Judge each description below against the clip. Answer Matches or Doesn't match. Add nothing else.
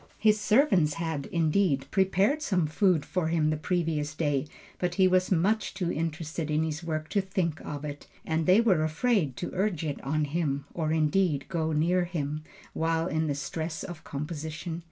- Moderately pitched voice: Matches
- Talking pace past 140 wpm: Matches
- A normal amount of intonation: Matches